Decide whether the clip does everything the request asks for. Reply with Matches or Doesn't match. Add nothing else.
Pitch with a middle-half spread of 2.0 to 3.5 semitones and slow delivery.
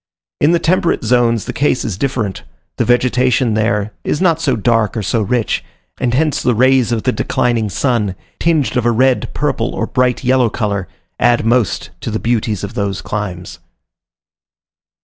Doesn't match